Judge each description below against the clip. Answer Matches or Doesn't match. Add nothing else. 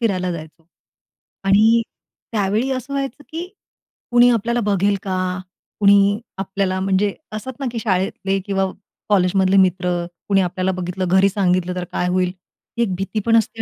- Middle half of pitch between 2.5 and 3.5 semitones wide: Matches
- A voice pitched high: Matches